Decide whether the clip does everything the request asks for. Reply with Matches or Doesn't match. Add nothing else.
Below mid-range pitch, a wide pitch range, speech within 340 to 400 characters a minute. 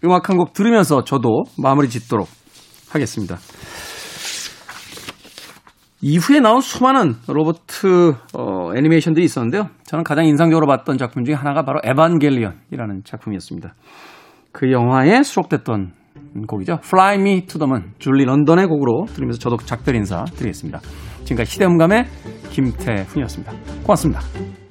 Doesn't match